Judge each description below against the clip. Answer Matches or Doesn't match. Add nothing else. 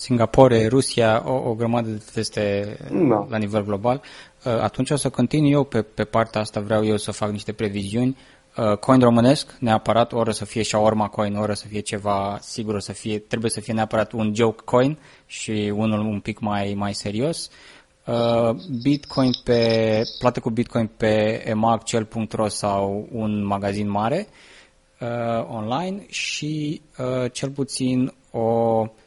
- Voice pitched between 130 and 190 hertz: Doesn't match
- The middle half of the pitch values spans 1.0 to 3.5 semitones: Matches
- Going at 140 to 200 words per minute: Matches